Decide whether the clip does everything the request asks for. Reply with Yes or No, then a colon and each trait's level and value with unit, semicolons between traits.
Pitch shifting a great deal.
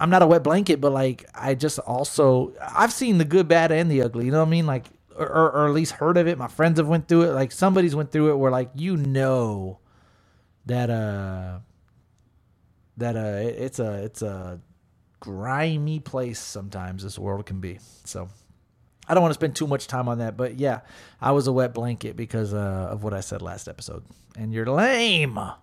Yes: wide, 6.9 semitones